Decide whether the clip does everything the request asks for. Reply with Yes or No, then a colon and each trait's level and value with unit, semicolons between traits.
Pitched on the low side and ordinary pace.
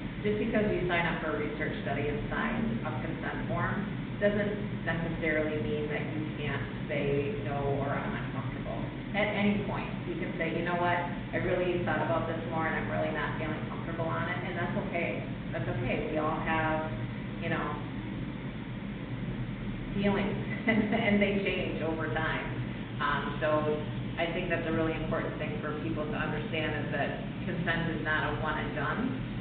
No: medium, 160 Hz; average, 175 wpm